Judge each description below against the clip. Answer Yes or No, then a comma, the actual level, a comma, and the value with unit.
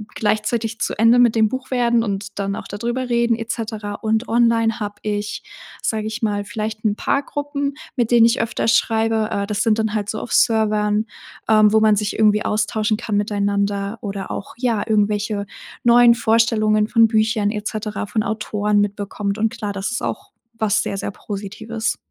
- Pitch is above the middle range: Yes, high, 215 Hz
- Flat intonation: Yes, narrow, 1.7 semitones